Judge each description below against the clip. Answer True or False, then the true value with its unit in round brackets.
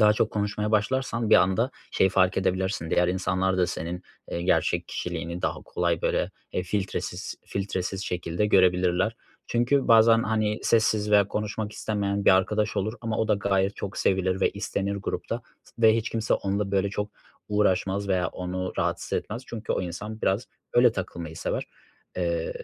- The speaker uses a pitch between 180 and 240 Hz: False (100 Hz)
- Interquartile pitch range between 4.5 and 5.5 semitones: False (2.7 semitones)